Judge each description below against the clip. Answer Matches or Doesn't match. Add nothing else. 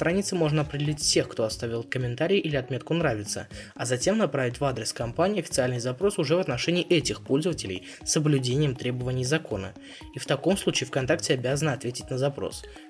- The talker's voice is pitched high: Doesn't match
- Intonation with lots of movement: Doesn't match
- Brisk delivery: Matches